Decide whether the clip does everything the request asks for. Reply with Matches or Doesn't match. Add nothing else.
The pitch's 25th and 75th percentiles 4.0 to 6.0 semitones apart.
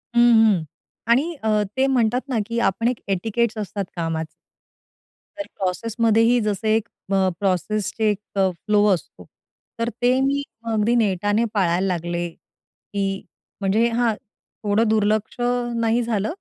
Doesn't match